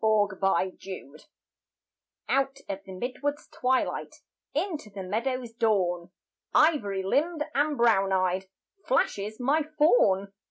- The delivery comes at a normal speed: No, slow, 120 wpm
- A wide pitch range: Yes, wide, 6.1 semitones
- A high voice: Yes, high, 220 Hz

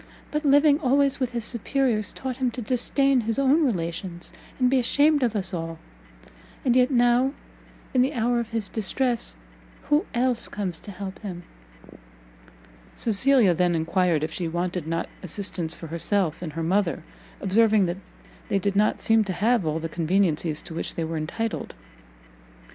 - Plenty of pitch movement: Yes, wide, 6.4 semitones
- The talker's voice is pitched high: Yes, high, 210 Hz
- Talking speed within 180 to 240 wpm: No, average, 165 wpm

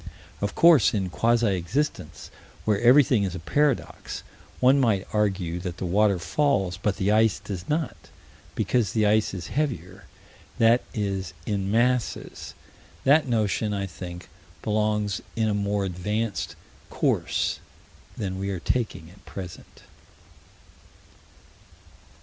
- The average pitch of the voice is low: Yes, low, 105 Hz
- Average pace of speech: No, slow, 125 wpm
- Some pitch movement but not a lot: Yes, average, 3.4 semitones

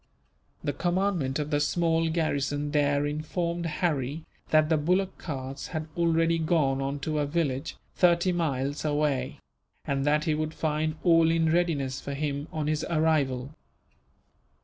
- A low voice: No, medium, 155 Hz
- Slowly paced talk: No, average, 150 wpm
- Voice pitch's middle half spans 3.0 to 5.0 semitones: No, narrow, 2.5 semitones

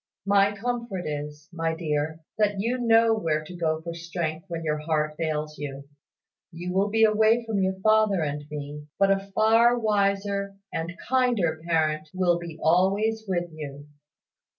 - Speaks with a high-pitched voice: No, medium, 175 Hz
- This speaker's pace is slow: No, average, 160 wpm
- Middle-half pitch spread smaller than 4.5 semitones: No, average, 5.0 semitones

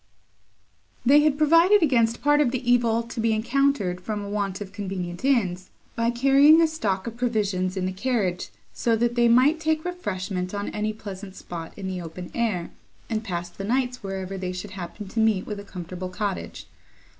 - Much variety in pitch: No, average, 4.7 semitones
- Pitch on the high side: Yes, high, 215 Hz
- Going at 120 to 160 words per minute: No, average, 190 wpm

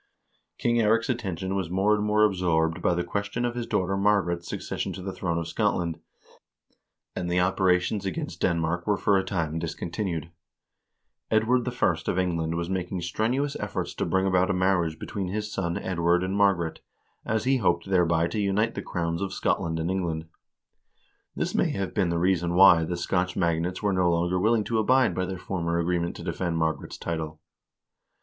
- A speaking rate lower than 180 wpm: No, average, 185 wpm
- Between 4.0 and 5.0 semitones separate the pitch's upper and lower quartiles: No, average, 3.0 semitones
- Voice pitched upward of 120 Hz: No, very low, 90 Hz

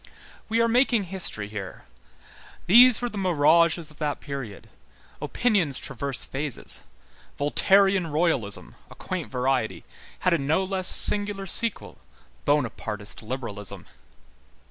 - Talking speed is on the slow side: Yes, slow, 115 wpm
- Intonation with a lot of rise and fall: Yes, wide, 6.4 semitones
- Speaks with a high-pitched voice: No, medium, 160 Hz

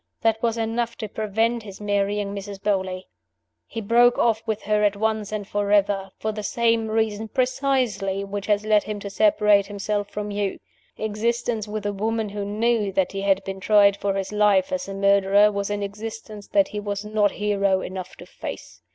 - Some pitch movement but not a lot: No, narrow, 1.7 semitones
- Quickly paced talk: No, average, 190 wpm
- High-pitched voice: Yes, high, 205 Hz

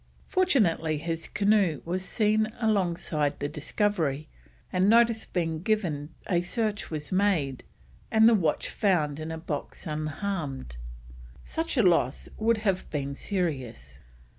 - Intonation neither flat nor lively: No, wide, 5.7 semitones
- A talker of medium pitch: Yes, medium, 175 Hz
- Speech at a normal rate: No, slow, 130 wpm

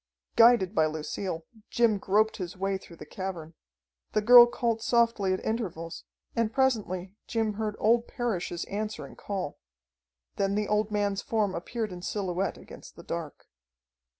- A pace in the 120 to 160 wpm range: Yes, average, 150 wpm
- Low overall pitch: No, high, 205 Hz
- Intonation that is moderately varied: Yes, average, 3.5 semitones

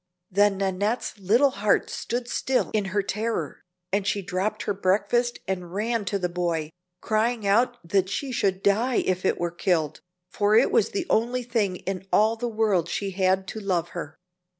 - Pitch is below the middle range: No, high, 200 Hz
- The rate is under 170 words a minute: No, average, 180 wpm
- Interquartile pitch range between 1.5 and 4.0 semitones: Yes, average, 3.3 semitones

